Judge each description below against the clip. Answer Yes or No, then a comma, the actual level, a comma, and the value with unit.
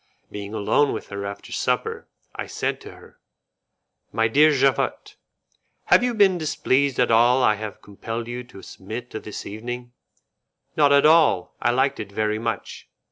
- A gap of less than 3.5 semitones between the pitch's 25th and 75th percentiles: No, average, 4.6 semitones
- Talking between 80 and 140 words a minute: No, average, 165 wpm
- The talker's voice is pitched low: Yes, low, 120 Hz